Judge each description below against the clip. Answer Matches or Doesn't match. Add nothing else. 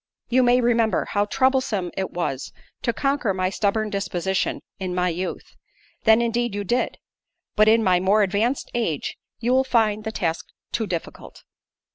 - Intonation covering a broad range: Doesn't match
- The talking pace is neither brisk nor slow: Matches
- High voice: Matches